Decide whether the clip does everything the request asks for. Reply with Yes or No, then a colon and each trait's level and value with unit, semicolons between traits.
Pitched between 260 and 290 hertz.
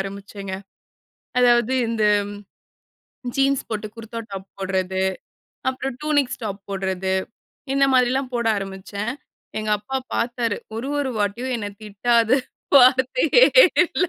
No: high, 230 Hz